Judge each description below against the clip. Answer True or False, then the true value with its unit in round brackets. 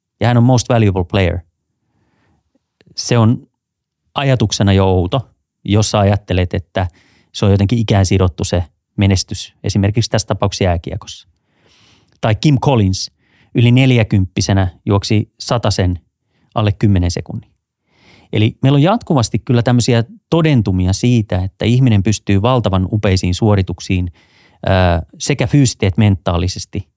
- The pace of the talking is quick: False (120 wpm)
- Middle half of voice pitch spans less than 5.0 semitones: True (3.8 semitones)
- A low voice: True (105 Hz)